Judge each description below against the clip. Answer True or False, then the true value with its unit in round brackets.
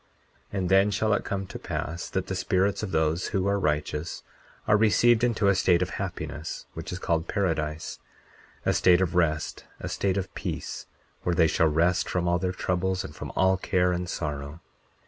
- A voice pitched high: False (90 Hz)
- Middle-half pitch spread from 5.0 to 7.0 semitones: False (2.7 semitones)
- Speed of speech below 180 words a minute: False (195 wpm)